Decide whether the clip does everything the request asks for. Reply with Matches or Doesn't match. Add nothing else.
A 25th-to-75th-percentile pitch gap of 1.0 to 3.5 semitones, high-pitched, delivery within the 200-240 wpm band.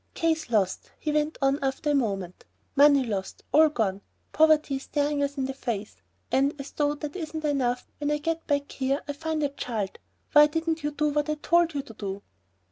Matches